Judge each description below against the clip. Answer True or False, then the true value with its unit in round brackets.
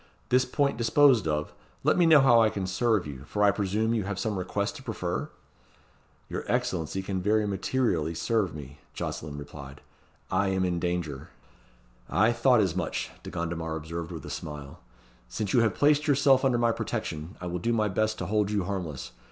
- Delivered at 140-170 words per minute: False (190 wpm)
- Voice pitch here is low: True (95 Hz)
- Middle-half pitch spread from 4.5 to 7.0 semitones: True (5.6 semitones)